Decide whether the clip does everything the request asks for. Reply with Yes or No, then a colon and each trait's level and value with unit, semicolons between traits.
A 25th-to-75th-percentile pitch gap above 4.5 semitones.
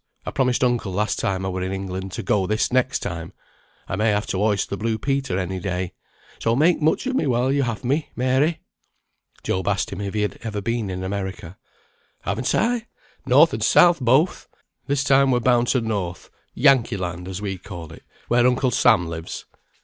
Yes: average, 5.3 semitones